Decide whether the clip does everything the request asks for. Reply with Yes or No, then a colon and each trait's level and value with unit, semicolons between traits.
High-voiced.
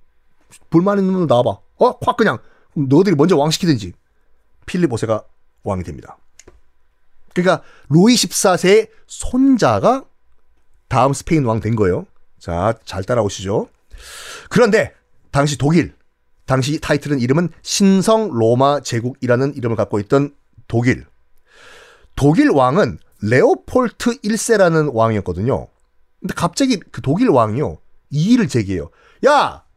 No: low, 135 Hz